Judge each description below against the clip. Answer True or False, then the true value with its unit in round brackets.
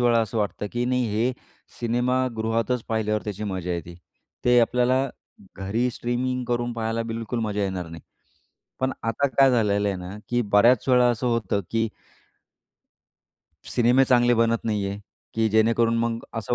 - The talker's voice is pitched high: False (115 Hz)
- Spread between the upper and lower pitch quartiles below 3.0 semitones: True (2.5 semitones)